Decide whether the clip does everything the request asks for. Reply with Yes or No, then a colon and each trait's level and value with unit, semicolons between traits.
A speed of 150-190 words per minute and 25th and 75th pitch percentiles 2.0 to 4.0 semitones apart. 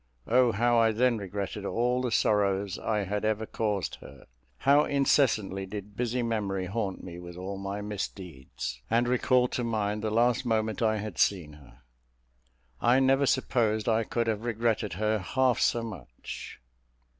Yes: average, 160 wpm; average, 3.4 semitones